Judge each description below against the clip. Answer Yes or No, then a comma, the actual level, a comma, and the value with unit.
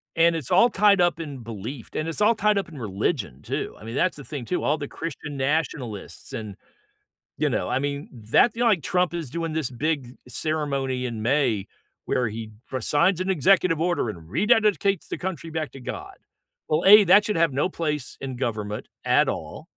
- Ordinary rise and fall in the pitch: No, wide, 6.0 semitones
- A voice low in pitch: No, medium, 150 Hz